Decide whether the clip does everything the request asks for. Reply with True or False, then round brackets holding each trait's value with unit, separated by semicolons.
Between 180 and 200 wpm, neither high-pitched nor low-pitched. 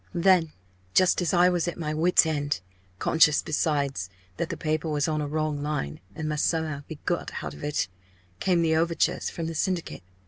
True (195 wpm; 155 Hz)